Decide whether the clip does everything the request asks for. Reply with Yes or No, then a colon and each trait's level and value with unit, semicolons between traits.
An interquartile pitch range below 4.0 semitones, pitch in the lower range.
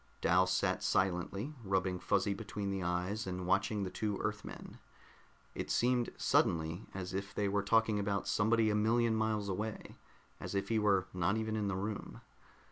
Yes: narrow, 2.6 semitones; low, 100 Hz